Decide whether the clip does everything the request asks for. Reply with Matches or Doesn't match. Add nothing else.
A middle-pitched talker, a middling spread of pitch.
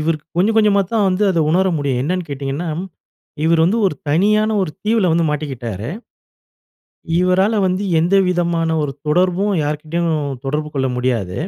Matches